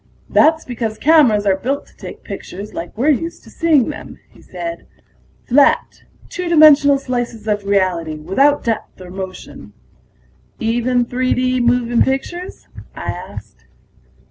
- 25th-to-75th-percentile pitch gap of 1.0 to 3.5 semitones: No, wide, 5.6 semitones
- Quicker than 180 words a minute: No, average, 140 wpm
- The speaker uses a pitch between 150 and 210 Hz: No, high, 245 Hz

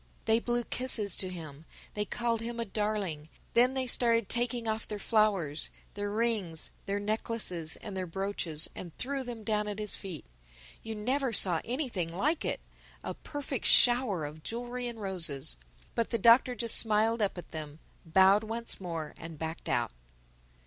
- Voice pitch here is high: Yes, high, 210 Hz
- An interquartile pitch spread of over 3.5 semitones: Yes, average, 4.7 semitones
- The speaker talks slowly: No, average, 165 wpm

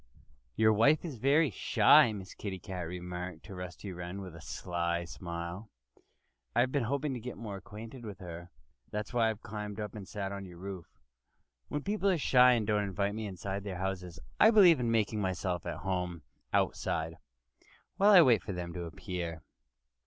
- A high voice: No, low, 100 Hz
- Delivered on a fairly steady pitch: No, average, 4.4 semitones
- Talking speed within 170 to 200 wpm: Yes, average, 180 wpm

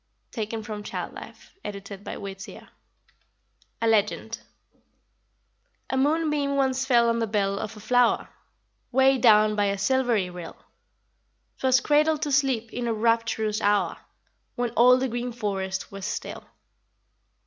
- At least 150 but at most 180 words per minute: No, slow, 135 wpm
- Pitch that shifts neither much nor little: Yes, average, 3.9 semitones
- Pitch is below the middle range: No, high, 230 Hz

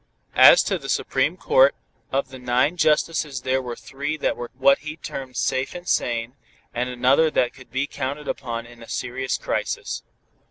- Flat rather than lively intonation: No, average, 3.3 semitones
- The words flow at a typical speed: Yes, average, 175 wpm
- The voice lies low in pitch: Yes, low, 130 Hz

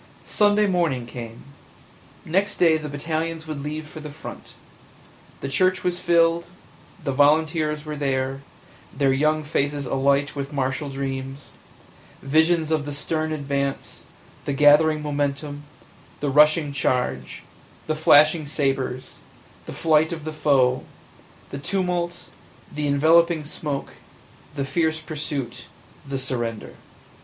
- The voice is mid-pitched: Yes, medium, 150 Hz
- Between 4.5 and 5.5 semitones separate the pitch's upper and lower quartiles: No, narrow, 2.4 semitones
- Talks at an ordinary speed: No, slow, 130 wpm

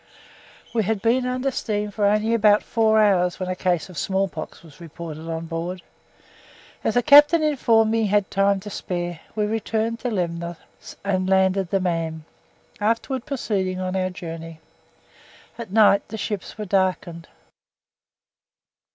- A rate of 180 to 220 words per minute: No, average, 150 wpm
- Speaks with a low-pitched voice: No, high, 195 Hz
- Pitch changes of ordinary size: Yes, average, 3.9 semitones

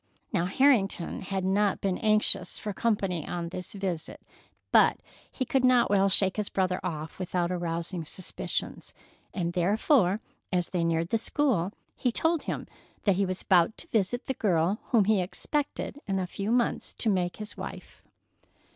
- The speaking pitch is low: No, high, 195 Hz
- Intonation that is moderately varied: Yes, average, 3.4 semitones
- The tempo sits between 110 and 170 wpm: Yes, average, 165 wpm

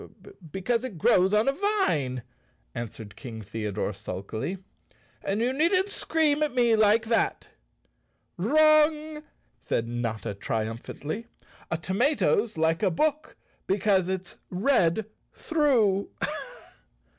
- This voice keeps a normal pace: No, slow, 115 wpm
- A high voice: Yes, high, 200 Hz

